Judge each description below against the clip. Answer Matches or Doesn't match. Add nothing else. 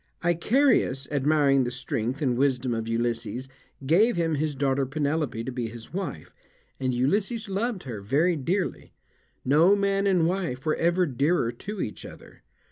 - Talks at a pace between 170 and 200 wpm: Doesn't match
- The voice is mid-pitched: Matches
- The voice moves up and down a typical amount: Doesn't match